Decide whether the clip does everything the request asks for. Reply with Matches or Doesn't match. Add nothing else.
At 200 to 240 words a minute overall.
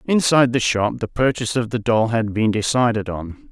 Matches